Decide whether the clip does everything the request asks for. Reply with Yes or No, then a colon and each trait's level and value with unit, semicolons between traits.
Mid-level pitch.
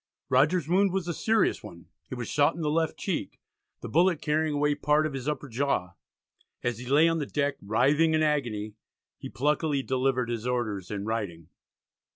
Yes: medium, 145 Hz